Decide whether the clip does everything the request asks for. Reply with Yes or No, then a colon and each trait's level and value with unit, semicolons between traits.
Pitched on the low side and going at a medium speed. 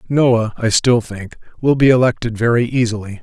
Yes: low, 115 Hz; average, 165 wpm